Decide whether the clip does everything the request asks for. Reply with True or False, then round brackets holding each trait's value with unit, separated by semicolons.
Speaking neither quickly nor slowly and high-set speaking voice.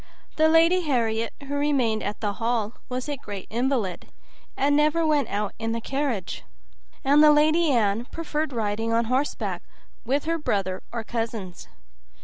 True (155 wpm; 245 Hz)